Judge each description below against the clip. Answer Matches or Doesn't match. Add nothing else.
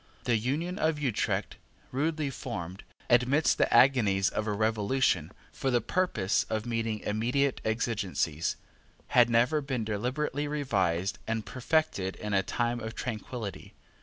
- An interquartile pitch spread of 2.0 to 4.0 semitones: Doesn't match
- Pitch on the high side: Doesn't match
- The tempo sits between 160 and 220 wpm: Doesn't match